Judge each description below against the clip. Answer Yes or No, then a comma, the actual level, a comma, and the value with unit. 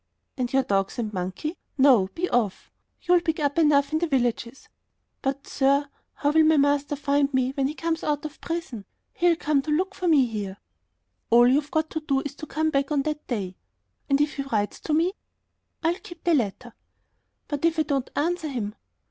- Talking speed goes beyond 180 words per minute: Yes, average, 200 wpm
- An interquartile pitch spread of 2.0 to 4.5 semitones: Yes, average, 3.7 semitones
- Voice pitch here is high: Yes, very high, 285 Hz